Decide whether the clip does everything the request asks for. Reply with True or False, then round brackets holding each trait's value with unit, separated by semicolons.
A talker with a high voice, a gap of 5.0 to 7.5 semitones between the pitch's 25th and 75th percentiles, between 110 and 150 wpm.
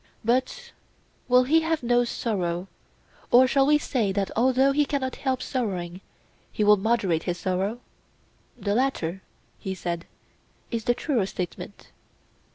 True (235 Hz; 5.4 semitones; 140 wpm)